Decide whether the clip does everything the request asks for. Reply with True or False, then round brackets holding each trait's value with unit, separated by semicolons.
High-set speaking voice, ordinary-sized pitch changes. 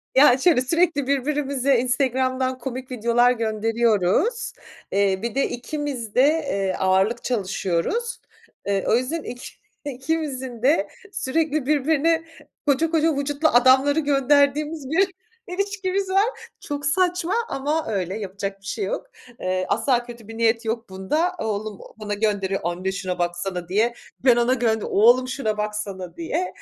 False (255 Hz; 5.9 semitones)